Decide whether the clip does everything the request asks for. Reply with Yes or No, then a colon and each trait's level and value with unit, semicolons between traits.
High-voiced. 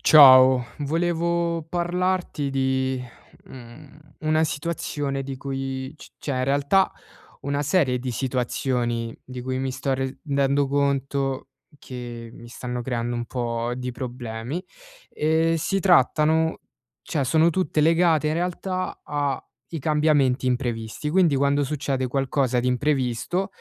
No: medium, 140 Hz